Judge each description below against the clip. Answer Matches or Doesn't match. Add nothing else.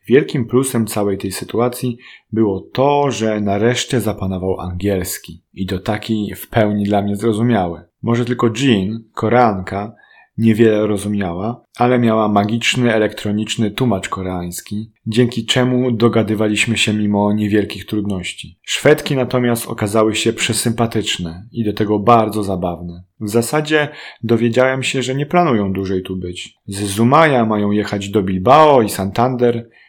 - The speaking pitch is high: Doesn't match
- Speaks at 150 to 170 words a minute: Doesn't match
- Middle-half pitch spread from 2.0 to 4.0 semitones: Matches